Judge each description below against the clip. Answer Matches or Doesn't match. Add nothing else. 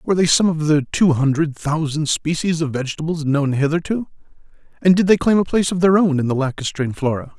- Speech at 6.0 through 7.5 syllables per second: Matches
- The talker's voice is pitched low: Doesn't match